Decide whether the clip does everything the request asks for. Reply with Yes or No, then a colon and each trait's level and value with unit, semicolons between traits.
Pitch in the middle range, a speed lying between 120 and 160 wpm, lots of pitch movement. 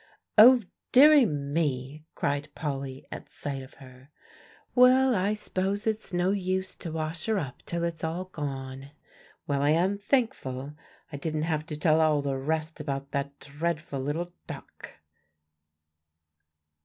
No: medium, 155 Hz; average, 145 wpm; average, 4.9 semitones